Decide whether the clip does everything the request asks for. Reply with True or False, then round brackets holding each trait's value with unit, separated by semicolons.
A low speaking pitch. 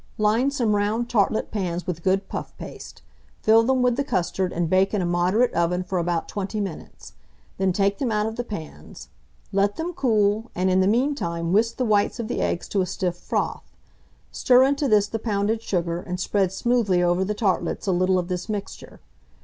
False (200 Hz)